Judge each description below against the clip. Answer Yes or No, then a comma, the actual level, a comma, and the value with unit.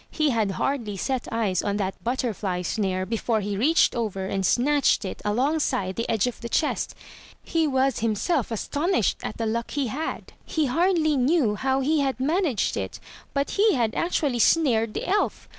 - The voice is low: No, high, 245 Hz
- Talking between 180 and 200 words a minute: Yes, average, 185 wpm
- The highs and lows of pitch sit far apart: Yes, wide, 5.8 semitones